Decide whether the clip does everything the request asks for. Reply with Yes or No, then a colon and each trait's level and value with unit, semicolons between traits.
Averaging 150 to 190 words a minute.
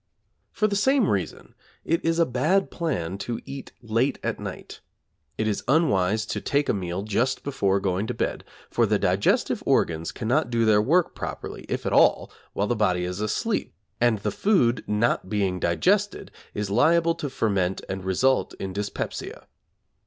Yes: average, 170 wpm